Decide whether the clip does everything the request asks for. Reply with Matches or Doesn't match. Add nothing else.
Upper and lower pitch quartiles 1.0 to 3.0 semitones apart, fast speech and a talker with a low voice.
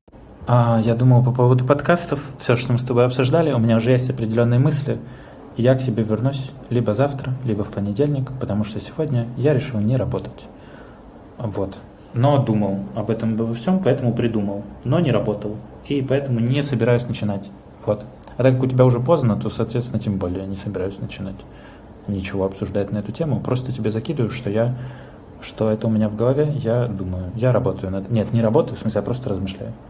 Doesn't match